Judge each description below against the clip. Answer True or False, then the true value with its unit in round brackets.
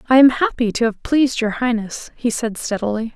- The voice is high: True (235 Hz)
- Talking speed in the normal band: False (210 wpm)